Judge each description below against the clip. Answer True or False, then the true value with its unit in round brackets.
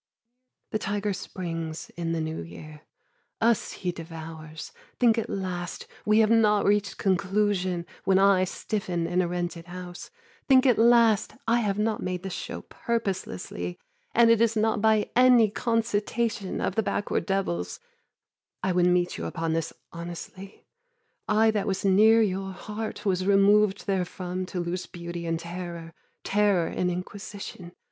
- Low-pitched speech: False (190 Hz)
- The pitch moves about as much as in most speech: True (3.4 semitones)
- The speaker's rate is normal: True (150 wpm)